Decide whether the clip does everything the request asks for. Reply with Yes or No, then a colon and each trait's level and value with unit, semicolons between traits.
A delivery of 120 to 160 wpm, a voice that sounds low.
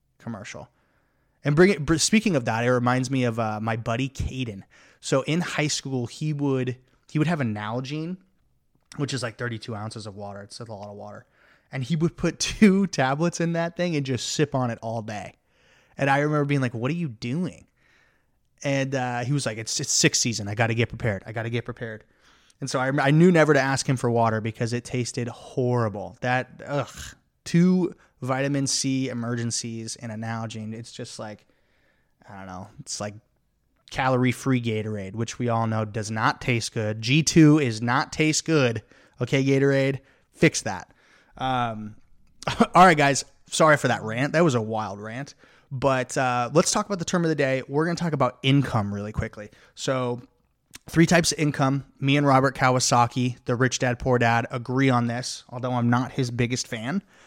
No: average, 195 wpm; low, 125 Hz